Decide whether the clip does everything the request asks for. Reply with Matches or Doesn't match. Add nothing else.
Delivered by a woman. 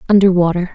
Matches